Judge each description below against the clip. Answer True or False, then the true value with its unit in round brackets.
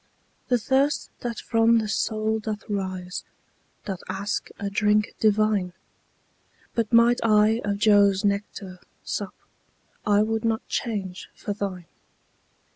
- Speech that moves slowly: True (120 wpm)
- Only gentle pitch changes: True (1.9 semitones)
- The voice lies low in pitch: False (210 Hz)